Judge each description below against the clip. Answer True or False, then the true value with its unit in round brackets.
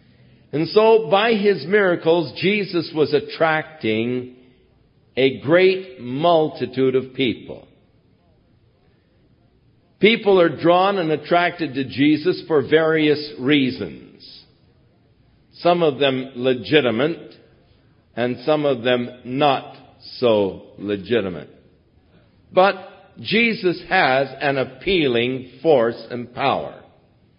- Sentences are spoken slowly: True (90 wpm)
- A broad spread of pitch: True (6.4 semitones)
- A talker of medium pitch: True (150 Hz)